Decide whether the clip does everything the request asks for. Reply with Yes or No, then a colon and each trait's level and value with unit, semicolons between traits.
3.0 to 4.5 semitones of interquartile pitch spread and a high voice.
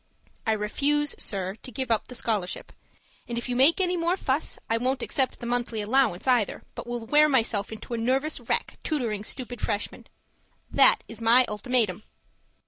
Yes: average, 3.3 semitones; high, 240 Hz